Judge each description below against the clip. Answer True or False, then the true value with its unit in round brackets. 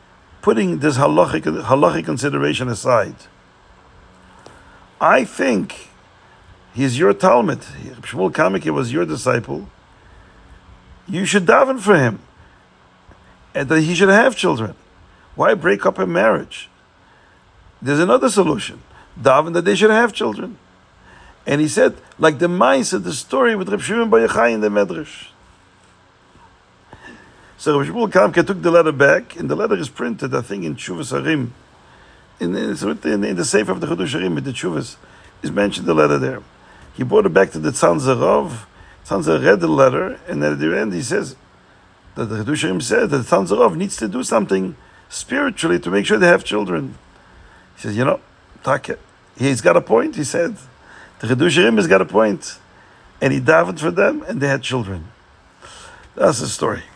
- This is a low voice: True (105 Hz)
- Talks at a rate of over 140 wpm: True (160 wpm)